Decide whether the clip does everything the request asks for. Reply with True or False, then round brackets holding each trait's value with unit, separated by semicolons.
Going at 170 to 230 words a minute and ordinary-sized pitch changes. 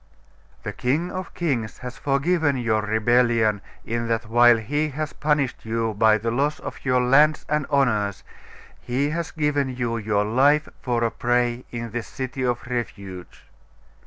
False (160 wpm; 4.0 semitones)